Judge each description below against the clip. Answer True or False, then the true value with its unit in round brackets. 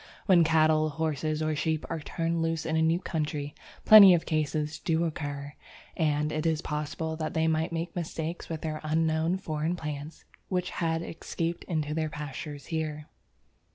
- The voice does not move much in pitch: True (1.3 semitones)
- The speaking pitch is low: False (160 Hz)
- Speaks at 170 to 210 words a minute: False (160 wpm)